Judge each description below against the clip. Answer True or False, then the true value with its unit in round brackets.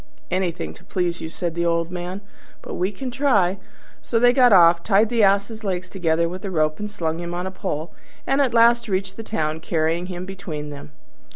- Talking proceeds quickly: True (210 wpm)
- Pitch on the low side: False (185 Hz)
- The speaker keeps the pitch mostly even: False (3.8 semitones)